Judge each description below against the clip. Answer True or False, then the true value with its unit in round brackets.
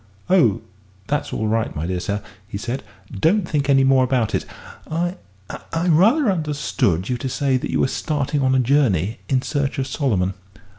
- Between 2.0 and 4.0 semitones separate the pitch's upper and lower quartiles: False (5.3 semitones)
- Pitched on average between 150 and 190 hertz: False (135 Hz)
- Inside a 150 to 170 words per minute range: False (185 wpm)